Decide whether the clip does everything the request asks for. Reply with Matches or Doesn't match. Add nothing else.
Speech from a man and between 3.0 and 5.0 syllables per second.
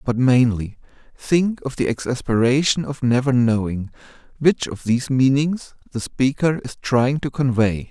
Matches